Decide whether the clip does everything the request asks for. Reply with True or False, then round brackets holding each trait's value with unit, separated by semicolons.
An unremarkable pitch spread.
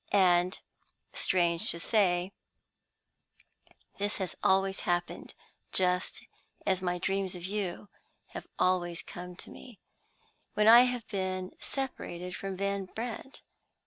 False (2.2 semitones)